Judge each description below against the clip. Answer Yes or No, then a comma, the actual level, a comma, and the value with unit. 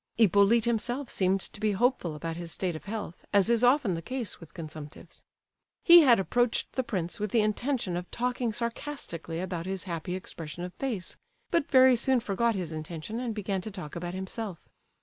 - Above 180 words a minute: Yes, average, 190 wpm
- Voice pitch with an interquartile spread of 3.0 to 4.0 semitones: No, average, 5.3 semitones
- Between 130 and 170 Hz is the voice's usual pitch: No, high, 200 Hz